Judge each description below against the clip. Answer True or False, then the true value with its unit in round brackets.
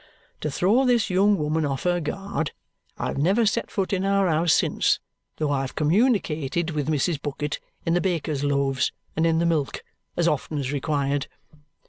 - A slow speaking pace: False (175 wpm)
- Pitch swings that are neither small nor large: True (4.3 semitones)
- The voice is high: False (160 Hz)